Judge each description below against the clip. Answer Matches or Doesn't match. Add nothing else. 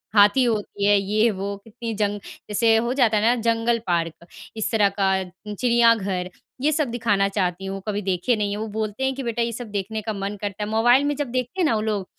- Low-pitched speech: Doesn't match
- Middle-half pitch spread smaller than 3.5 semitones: Matches